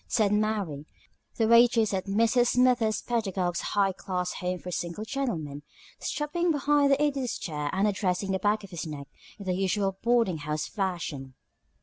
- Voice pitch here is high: Yes, high, 200 Hz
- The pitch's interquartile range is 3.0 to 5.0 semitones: Yes, average, 4.6 semitones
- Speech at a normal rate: Yes, average, 160 wpm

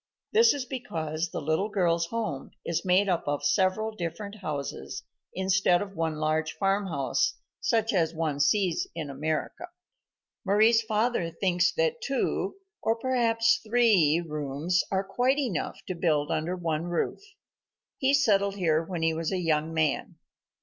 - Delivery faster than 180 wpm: No, average, 150 wpm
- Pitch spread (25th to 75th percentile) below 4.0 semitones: No, average, 5.3 semitones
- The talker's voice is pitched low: No, medium, 180 Hz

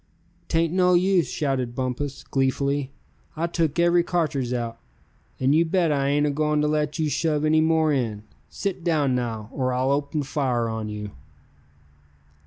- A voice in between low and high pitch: Yes, medium, 145 Hz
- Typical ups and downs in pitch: Yes, average, 4.0 semitones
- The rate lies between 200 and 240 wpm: No, average, 160 wpm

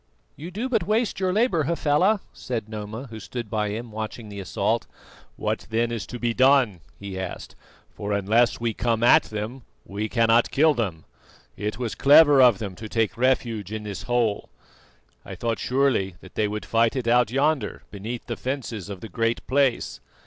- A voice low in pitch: Yes, low, 115 Hz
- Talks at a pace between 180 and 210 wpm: Yes, average, 185 wpm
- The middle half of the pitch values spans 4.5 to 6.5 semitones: No, average, 3.9 semitones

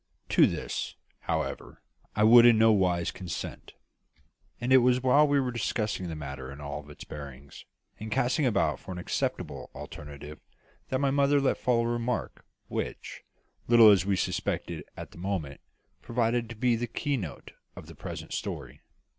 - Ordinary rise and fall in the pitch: No, wide, 6.5 semitones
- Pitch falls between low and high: No, low, 110 Hz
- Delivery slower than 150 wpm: No, average, 170 wpm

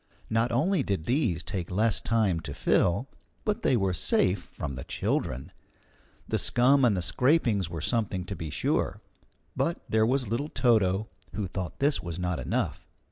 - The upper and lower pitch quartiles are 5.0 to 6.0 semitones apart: Yes, wide, 5.6 semitones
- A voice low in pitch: Yes, low, 105 Hz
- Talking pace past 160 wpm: Yes, average, 170 wpm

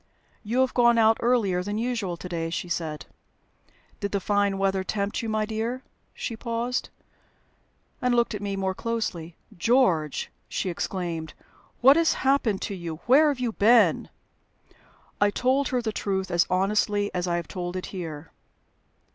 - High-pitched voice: Yes, high, 205 Hz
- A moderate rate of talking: Yes, average, 165 wpm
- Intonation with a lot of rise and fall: No, average, 4.6 semitones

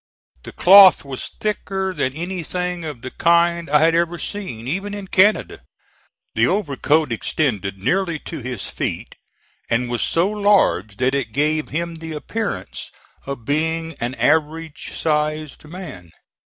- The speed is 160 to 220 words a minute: No, average, 140 wpm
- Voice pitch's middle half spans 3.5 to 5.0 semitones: Yes, average, 4.5 semitones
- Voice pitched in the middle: Yes, medium, 160 Hz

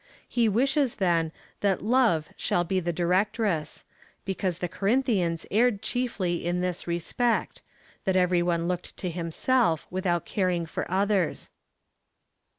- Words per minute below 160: Yes, slow, 135 wpm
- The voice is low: No, medium, 185 Hz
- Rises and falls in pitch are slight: No, average, 3.7 semitones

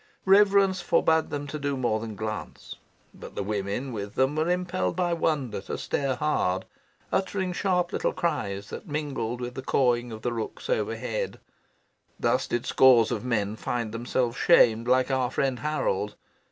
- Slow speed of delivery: No, average, 165 wpm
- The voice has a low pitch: Yes, low, 130 Hz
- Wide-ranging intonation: Yes, wide, 6.2 semitones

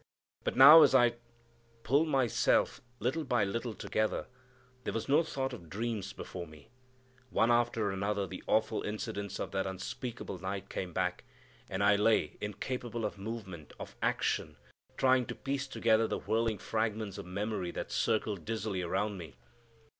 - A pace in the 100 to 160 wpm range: Yes, average, 155 wpm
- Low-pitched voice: Yes, low, 110 Hz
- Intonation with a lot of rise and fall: No, average, 3.5 semitones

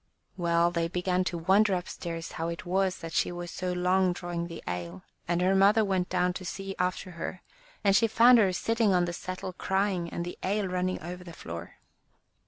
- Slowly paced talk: No, average, 200 wpm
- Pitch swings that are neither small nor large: No, narrow, 1.9 semitones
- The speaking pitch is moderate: Yes, medium, 180 Hz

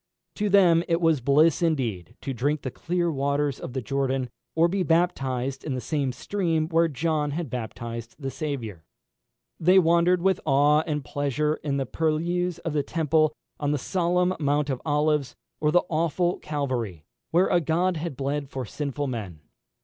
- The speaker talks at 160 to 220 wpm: Yes, average, 170 wpm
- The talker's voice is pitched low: No, medium, 150 Hz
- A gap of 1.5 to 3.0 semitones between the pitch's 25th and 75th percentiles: No, average, 3.7 semitones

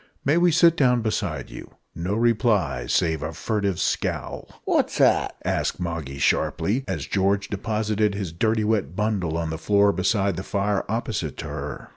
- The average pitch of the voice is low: Yes, low, 100 Hz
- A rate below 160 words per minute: No, average, 165 wpm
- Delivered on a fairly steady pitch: No, average, 4.7 semitones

